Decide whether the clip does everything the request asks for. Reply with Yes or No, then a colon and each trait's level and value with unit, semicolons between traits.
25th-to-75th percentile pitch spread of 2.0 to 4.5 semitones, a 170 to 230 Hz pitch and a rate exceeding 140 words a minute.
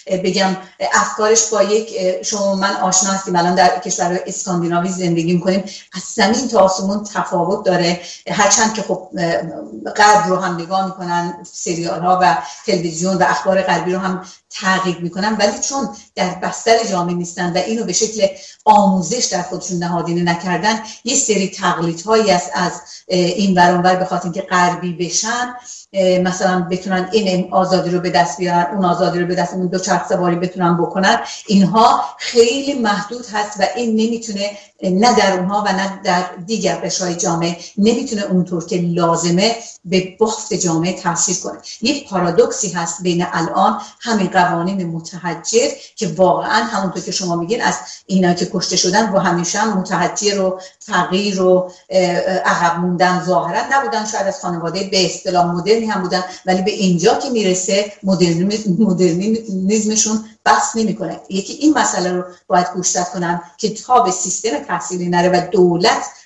Yes: narrow, 2.6 semitones; medium, 185 Hz; fast, 155 wpm